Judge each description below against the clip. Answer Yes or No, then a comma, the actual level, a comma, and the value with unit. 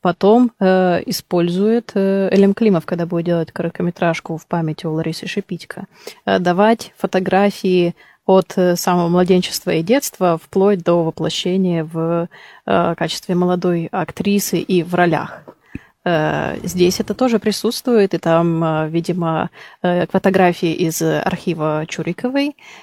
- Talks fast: No, average, 130 wpm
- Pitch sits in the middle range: Yes, medium, 180 Hz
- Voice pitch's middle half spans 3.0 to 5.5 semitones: No, narrow, 2.5 semitones